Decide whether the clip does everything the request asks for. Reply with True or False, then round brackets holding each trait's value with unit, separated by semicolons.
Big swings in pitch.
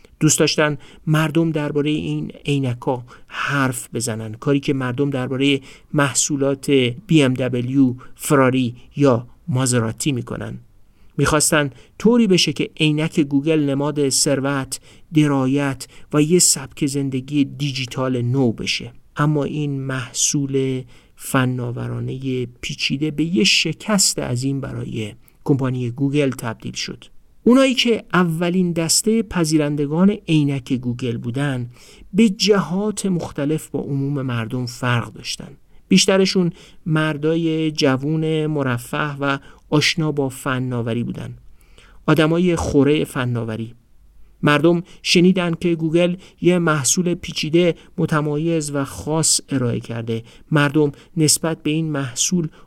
False (3.7 semitones)